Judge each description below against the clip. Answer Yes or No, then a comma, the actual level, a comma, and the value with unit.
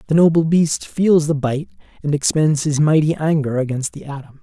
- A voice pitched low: No, medium, 150 Hz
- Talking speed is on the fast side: No, average, 190 wpm